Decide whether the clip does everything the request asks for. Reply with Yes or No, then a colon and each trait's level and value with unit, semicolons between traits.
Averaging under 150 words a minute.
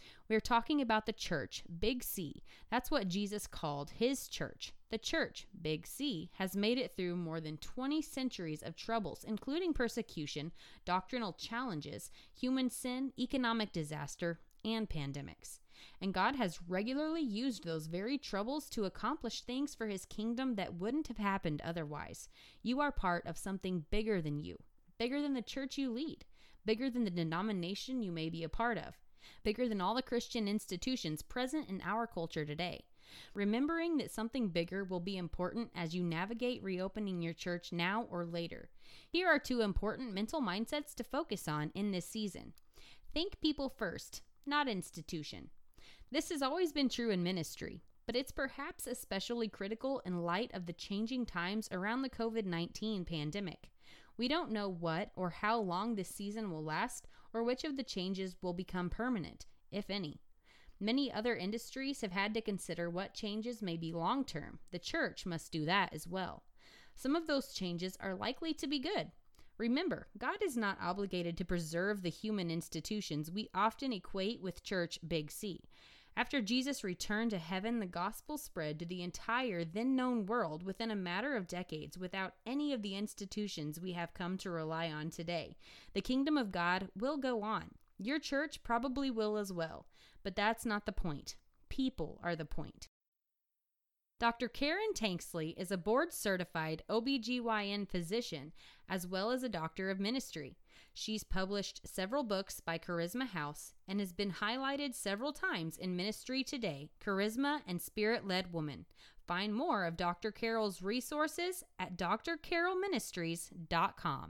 No: average, 165 wpm